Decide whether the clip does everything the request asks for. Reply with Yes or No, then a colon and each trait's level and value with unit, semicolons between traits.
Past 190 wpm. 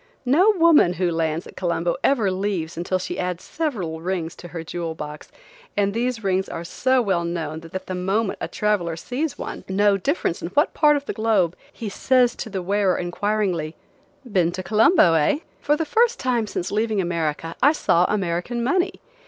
No: average, 185 wpm